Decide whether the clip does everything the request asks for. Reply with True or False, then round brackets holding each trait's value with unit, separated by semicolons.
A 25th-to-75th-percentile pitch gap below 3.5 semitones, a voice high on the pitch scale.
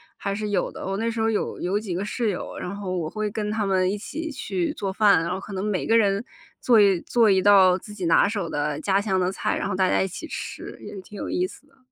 True (2.4 semitones; 200 Hz)